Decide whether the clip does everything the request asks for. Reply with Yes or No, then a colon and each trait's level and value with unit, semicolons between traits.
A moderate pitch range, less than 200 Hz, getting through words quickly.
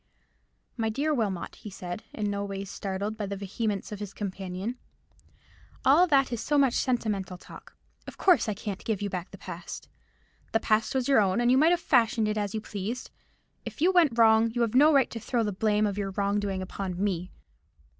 No: average, 3.5 semitones; high, 215 Hz; fast, 210 wpm